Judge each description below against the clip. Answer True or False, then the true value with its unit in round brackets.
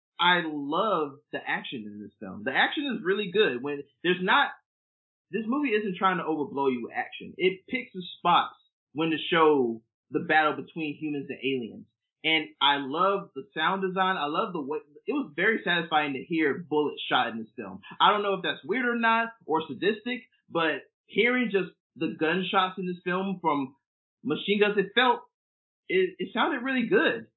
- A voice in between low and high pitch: True (170 Hz)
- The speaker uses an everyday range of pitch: False (6.1 semitones)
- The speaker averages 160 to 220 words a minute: True (190 wpm)